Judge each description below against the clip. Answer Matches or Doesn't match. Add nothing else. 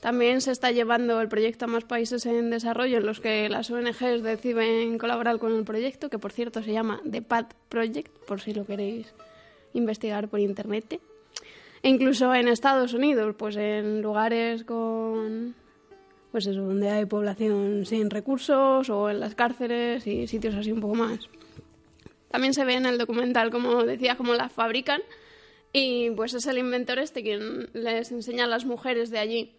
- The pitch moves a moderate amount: Doesn't match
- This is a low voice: Doesn't match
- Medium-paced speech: Matches